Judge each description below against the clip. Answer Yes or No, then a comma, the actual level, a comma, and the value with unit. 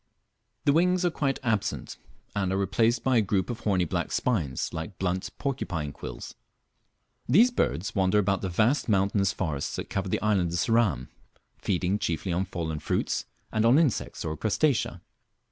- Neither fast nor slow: Yes, average, 165 wpm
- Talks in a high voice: No, low, 100 Hz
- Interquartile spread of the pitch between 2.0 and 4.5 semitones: No, average, 4.9 semitones